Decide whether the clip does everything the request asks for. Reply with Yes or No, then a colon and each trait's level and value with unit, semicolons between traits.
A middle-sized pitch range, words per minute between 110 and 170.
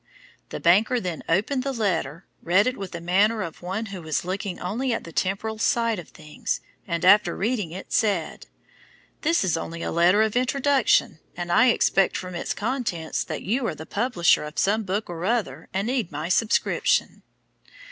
No: average, 4.8 semitones; average, 185 wpm